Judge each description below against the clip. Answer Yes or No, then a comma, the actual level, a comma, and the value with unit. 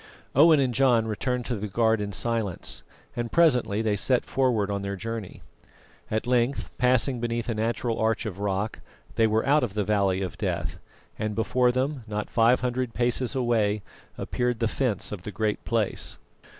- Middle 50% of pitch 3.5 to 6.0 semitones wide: No, average, 2.8 semitones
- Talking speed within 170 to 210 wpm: Yes, average, 175 wpm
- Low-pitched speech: Yes, low, 115 Hz